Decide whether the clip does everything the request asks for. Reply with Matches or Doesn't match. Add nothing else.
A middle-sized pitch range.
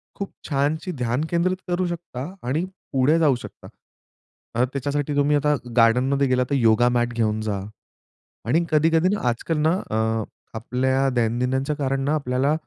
Matches